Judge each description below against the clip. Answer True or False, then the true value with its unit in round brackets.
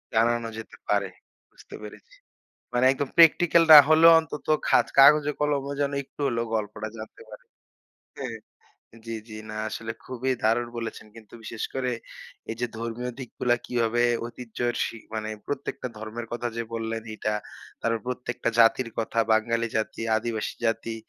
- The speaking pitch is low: True (115 Hz)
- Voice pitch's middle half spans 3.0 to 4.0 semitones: False (2.5 semitones)